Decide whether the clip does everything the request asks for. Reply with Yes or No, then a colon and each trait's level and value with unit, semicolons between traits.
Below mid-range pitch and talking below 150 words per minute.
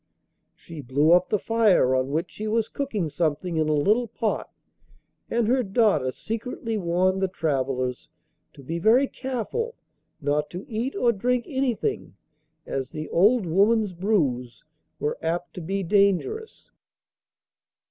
No: high, 190 Hz; average, 140 wpm